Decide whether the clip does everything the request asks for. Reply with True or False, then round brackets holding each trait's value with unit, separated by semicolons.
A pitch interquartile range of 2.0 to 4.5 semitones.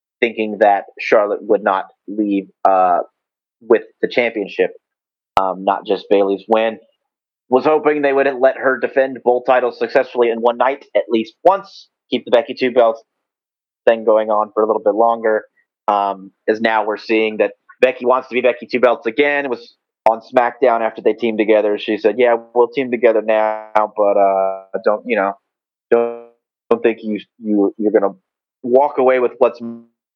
True (3.1 semitones)